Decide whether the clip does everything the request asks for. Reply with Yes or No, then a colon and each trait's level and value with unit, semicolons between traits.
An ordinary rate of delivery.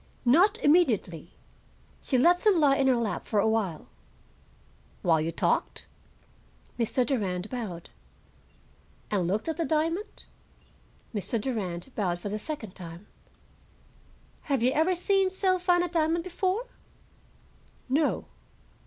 No: slow, 125 wpm